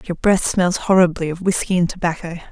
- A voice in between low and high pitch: Yes, medium, 175 Hz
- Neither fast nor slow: Yes, average, 190 wpm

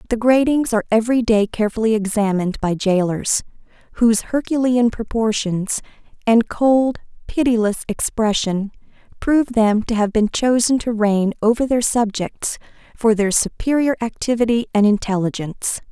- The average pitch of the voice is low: No, high, 225 Hz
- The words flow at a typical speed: No, slow, 125 wpm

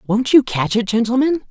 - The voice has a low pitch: No, high, 240 Hz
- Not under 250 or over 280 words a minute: No, average, 200 wpm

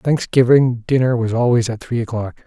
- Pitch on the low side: Yes, low, 120 Hz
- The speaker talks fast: No, average, 170 wpm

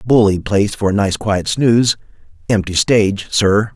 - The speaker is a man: Yes, male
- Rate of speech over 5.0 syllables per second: No, 4.9 syllables/s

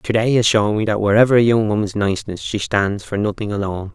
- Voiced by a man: Yes, male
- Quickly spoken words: Yes, fast, 245 wpm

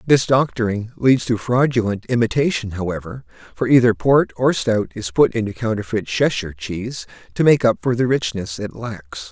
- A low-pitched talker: Yes, low, 115 Hz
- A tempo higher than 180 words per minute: No, average, 165 wpm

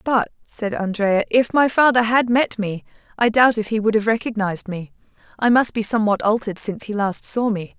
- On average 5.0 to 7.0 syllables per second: Yes, 5.5 syllables/s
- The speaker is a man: No, female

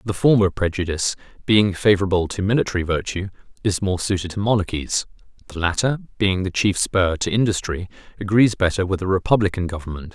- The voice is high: No, very low, 95 Hz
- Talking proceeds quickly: No, average, 160 wpm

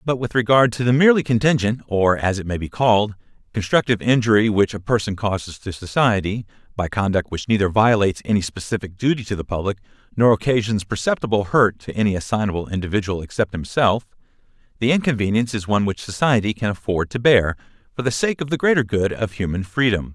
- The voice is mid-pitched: No, low, 110 Hz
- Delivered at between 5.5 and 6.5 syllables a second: Yes, 6.3 syllables/s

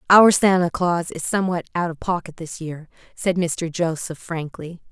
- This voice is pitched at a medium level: Yes, medium, 170 Hz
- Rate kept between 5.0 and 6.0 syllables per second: No, 4.6 syllables/s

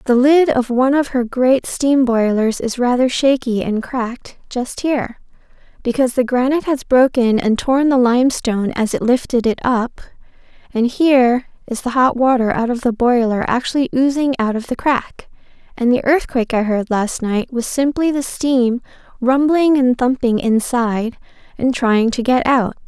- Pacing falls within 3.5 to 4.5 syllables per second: No, 4.8 syllables/s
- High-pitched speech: Yes, very high, 250 Hz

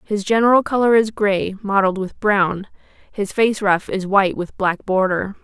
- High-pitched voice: Yes, high, 200 Hz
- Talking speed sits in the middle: Yes, average, 175 wpm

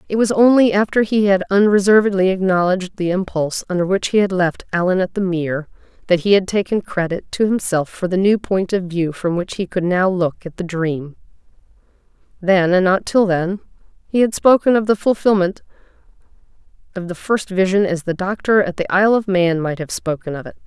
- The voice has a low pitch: No, high, 190 Hz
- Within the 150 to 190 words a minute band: No, average, 200 wpm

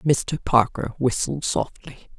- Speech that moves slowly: Yes, slow, 110 wpm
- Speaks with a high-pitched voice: No, low, 135 Hz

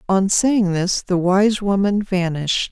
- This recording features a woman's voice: Yes, female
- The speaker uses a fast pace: No, average, 155 wpm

